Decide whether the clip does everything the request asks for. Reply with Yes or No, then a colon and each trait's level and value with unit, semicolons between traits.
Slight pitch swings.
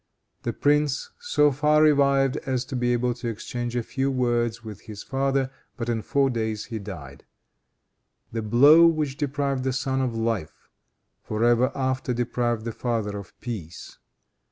No: average, 3.0 semitones